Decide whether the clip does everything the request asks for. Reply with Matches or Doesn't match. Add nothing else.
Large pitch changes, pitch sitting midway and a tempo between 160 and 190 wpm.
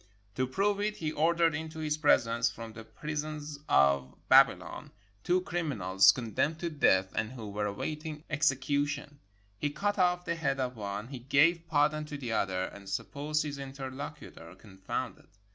Matches